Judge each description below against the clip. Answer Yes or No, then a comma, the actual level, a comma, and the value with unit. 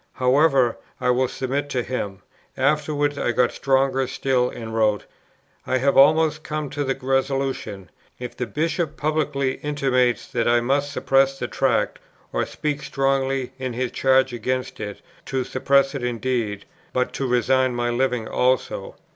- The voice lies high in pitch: No, low, 130 Hz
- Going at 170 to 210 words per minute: No, average, 155 wpm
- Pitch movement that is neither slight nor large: No, narrow, 2.0 semitones